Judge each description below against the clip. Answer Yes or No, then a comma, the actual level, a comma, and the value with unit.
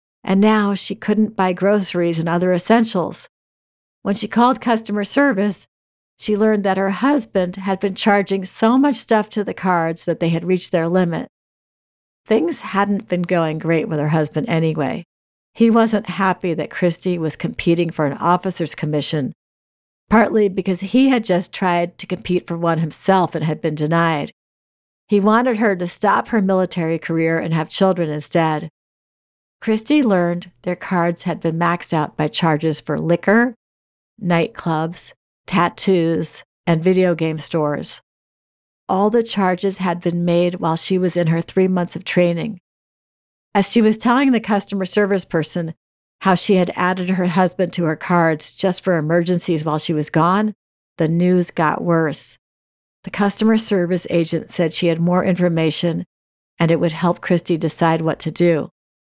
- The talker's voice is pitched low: No, medium, 180 Hz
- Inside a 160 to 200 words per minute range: Yes, average, 165 wpm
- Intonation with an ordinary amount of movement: Yes, average, 3.4 semitones